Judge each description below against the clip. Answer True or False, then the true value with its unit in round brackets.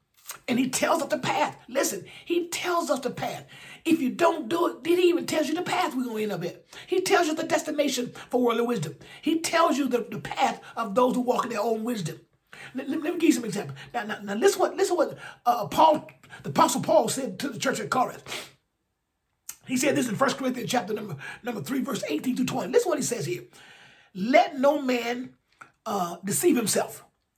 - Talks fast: True (235 wpm)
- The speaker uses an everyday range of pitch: False (5.8 semitones)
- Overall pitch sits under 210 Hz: False (255 Hz)